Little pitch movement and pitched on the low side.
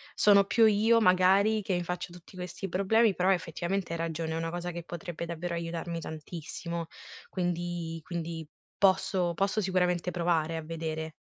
No: narrow, 2.3 semitones; medium, 175 Hz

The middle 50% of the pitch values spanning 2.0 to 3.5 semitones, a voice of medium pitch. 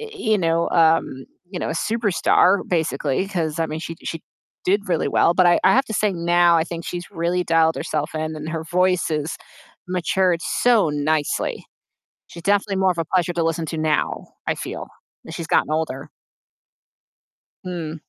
Yes: narrow, 2.4 semitones; medium, 170 Hz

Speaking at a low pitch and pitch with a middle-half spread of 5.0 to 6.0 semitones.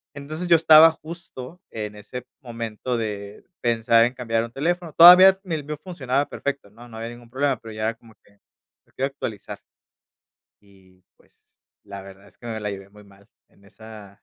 Yes: low, 115 Hz; wide, 5.5 semitones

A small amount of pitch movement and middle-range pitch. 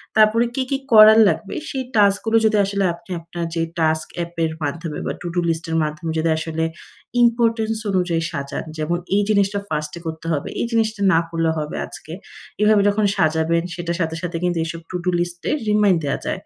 No: average, 4.5 semitones; medium, 175 Hz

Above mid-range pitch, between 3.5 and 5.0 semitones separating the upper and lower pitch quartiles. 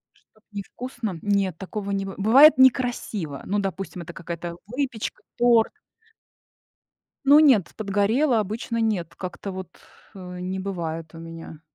Yes: high, 200 Hz; average, 4.4 semitones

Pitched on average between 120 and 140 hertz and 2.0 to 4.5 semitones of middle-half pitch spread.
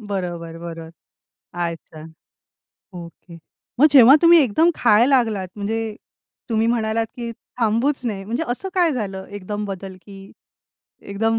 No: high, 210 Hz; average, 4.0 semitones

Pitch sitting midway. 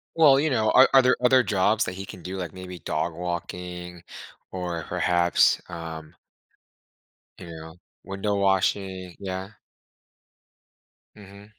No: very low, 95 Hz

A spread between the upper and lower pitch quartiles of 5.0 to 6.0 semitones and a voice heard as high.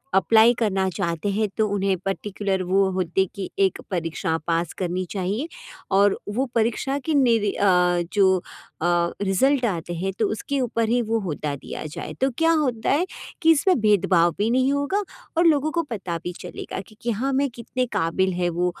Yes: wide, 5.4 semitones; high, 200 Hz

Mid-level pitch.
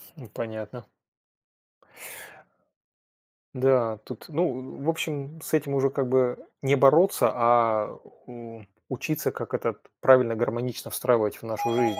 No: low, 125 Hz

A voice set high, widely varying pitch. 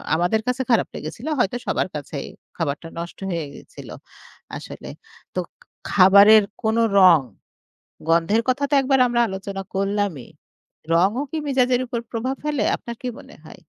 Yes: high, 205 Hz; wide, 5.8 semitones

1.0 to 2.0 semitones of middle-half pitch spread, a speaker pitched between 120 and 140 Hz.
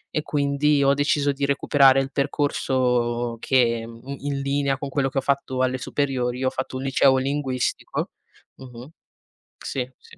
Yes: narrow, 1.6 semitones; low, 135 Hz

